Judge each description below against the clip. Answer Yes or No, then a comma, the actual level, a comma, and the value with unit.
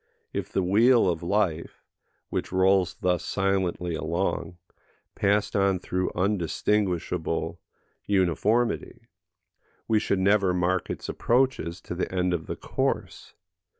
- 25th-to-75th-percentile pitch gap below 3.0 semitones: Yes, narrow, 2.5 semitones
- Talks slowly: Yes, slow, 115 wpm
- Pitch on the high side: No, very low, 95 Hz